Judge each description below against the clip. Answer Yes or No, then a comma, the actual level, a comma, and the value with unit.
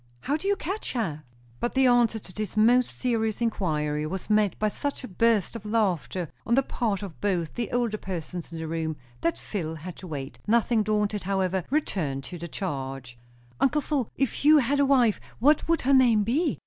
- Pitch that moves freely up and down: Yes, wide, 6.1 semitones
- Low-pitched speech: No, high, 210 Hz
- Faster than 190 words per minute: Yes, average, 200 wpm